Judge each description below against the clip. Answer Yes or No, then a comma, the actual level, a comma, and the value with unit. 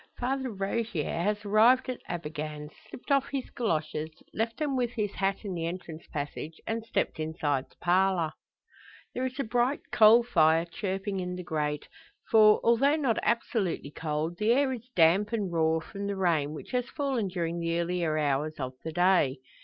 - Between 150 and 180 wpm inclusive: Yes, average, 175 wpm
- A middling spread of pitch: No, wide, 6.3 semitones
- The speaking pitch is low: No, high, 190 Hz